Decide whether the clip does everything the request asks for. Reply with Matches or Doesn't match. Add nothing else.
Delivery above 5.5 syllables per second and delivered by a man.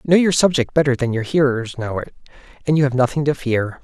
Matches